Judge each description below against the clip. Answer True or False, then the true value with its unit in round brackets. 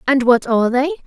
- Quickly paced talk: True (225 wpm)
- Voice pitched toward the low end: False (260 Hz)